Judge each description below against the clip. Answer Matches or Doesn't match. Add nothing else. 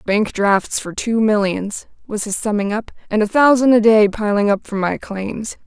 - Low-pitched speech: Doesn't match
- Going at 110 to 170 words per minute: Doesn't match